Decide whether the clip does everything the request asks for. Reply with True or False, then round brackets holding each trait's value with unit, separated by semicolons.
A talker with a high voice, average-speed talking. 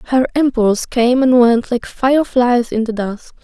True (245 Hz; 175 wpm)